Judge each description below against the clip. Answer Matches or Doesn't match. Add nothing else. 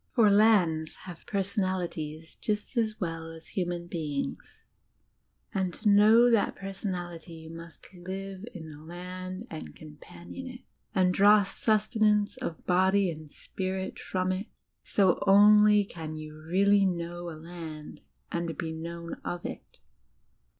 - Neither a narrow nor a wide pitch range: Matches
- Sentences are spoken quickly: Doesn't match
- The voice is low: Doesn't match